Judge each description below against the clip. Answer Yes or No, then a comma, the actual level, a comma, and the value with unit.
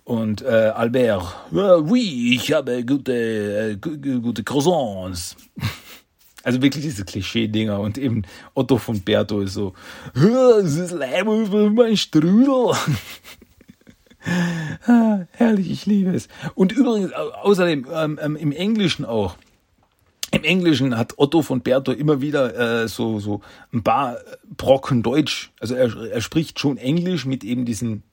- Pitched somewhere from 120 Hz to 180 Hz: Yes, medium, 140 Hz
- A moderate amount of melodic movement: No, wide, 7.8 semitones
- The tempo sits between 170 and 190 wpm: No, average, 140 wpm